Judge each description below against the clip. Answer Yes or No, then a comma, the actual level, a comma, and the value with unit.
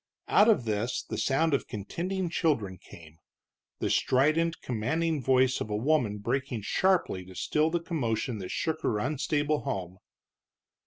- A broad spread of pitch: Yes, wide, 6.9 semitones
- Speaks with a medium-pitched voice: No, low, 130 Hz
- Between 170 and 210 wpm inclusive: No, average, 150 wpm